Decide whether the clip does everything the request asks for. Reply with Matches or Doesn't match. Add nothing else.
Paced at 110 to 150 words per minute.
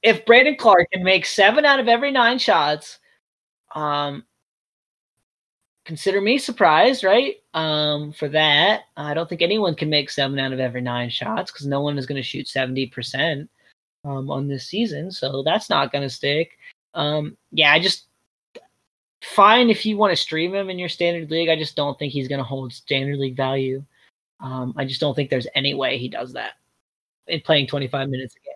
Doesn't match